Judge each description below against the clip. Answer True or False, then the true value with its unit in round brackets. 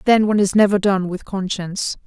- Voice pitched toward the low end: False (195 Hz)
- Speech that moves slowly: False (205 wpm)